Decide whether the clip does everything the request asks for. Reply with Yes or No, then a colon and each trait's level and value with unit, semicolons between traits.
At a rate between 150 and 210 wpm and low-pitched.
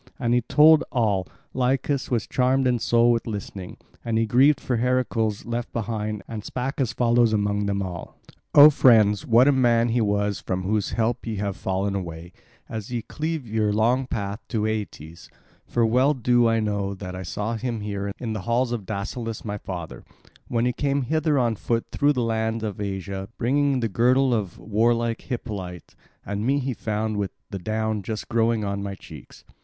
Yes: average, 190 wpm; low, 110 Hz